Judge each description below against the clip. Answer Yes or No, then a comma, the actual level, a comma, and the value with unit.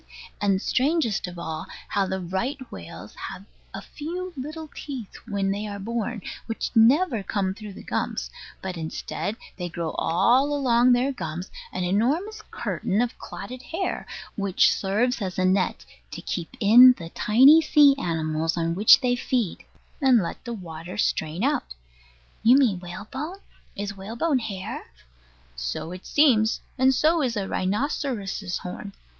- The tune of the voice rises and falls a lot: Yes, wide, 5.8 semitones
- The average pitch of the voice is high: Yes, high, 210 Hz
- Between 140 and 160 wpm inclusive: Yes, average, 150 wpm